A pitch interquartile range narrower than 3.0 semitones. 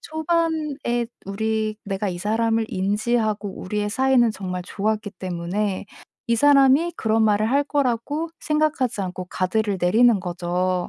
No: average, 5.1 semitones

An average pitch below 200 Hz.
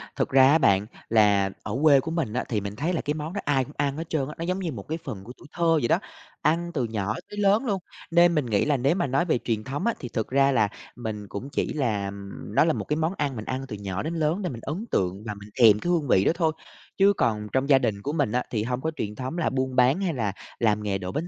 Yes: low, 135 Hz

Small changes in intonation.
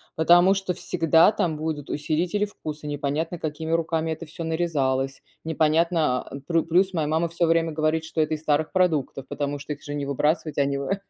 Yes: narrow, 2.0 semitones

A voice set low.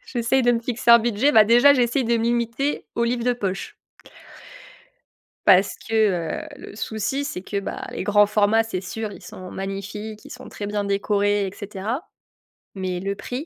No: high, 220 Hz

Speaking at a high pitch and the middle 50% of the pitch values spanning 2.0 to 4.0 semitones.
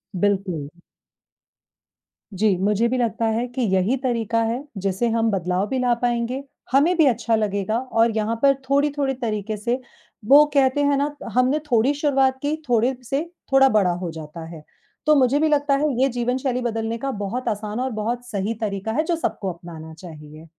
No: high, 235 Hz; average, 4.8 semitones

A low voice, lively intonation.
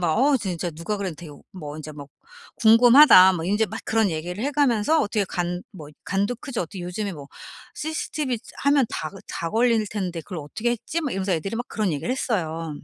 No: high, 200 Hz; wide, 5.9 semitones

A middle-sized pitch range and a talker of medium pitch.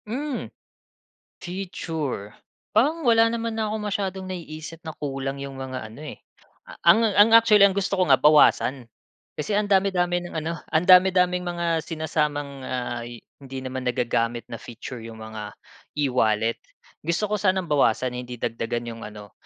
No: wide, 7.2 semitones; medium, 155 Hz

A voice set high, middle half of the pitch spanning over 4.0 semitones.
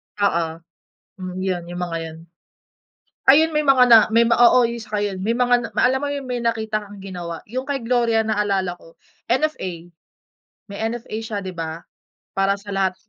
Yes: high, 215 Hz; average, 4.4 semitones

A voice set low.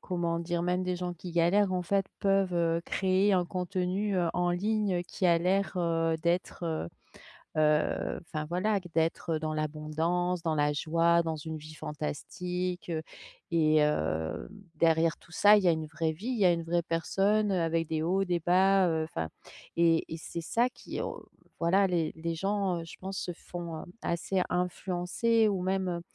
No: medium, 175 Hz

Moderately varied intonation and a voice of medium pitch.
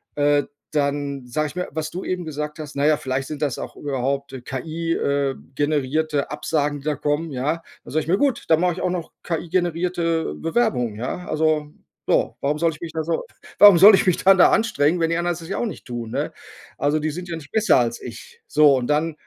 Yes: average, 3.0 semitones; medium, 155 Hz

